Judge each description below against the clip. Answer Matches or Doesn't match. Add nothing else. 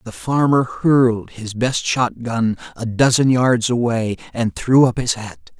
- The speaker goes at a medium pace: Matches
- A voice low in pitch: Matches